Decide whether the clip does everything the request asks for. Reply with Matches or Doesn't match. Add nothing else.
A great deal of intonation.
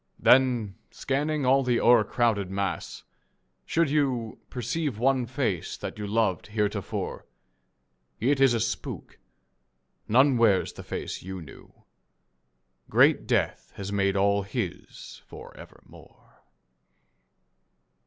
Doesn't match